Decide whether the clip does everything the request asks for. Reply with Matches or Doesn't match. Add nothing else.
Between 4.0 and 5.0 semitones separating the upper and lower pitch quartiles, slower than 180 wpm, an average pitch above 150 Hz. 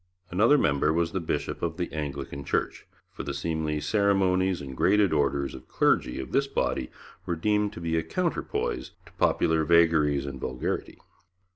Doesn't match